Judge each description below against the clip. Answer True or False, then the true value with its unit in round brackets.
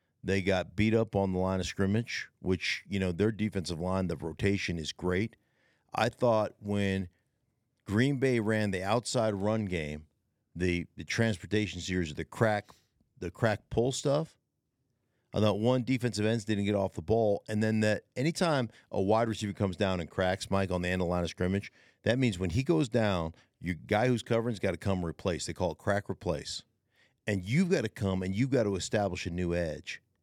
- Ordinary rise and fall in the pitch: True (3.8 semitones)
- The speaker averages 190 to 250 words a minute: True (200 wpm)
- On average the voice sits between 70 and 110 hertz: True (100 Hz)